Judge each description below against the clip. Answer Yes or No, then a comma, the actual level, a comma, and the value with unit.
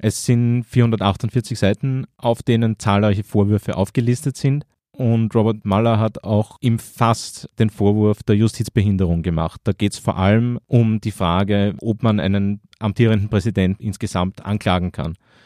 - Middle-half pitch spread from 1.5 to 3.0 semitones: Yes, narrow, 2.6 semitones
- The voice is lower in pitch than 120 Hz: Yes, low, 110 Hz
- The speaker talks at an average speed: Yes, average, 145 wpm